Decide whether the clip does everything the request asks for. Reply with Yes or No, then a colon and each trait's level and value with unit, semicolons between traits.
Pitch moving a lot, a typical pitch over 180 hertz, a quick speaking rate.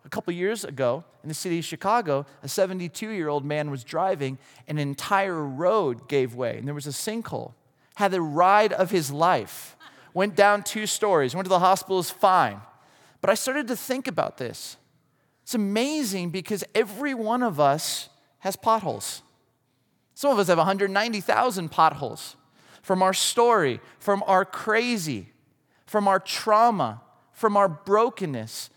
No: wide, 6.1 semitones; high, 190 Hz; average, 160 wpm